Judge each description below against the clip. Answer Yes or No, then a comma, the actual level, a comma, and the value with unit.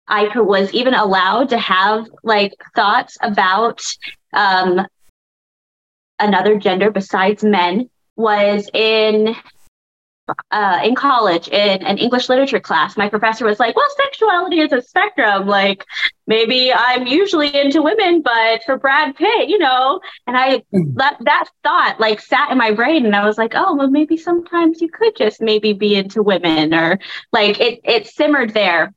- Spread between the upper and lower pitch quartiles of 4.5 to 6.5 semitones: Yes, wide, 5.5 semitones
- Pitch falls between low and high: No, high, 220 Hz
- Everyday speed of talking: Yes, average, 160 wpm